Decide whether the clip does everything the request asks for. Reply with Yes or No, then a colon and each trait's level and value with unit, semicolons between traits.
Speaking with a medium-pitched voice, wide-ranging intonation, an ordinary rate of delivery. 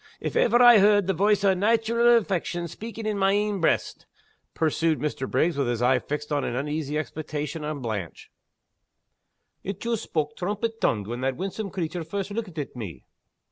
Yes: medium, 175 Hz; wide, 5.9 semitones; average, 175 wpm